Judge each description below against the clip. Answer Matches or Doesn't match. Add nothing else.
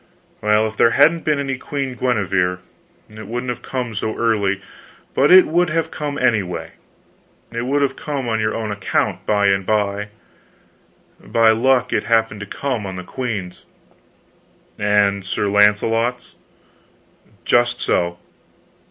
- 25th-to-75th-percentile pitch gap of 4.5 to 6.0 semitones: Doesn't match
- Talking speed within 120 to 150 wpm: Matches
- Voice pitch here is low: Matches